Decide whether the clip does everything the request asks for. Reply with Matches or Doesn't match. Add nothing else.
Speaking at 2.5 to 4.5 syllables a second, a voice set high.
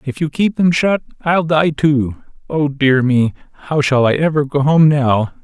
Doesn't match